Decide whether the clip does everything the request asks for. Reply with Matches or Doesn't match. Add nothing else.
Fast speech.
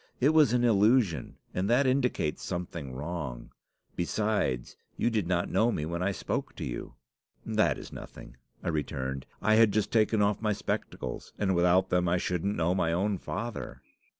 Doesn't match